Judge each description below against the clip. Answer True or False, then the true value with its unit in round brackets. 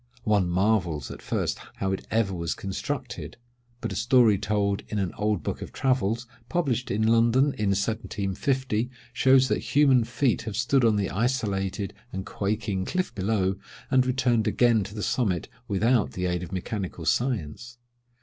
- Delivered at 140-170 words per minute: True (160 wpm)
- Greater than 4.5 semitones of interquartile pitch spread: False (4.1 semitones)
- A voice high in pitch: False (105 Hz)